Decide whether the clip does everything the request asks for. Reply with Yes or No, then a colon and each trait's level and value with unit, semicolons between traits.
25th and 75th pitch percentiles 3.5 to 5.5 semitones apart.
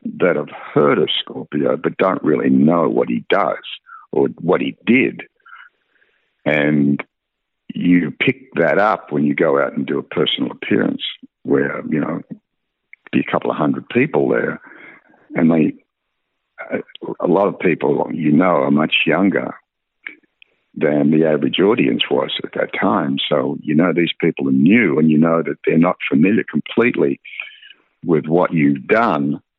No: average, 2.8 semitones